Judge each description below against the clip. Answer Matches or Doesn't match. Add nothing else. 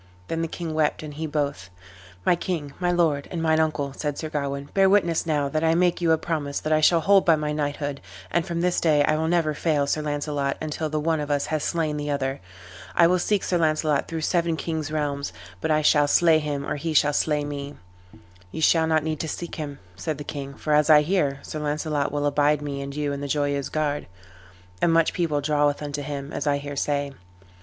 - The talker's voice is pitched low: Doesn't match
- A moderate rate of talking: Doesn't match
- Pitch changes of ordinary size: Doesn't match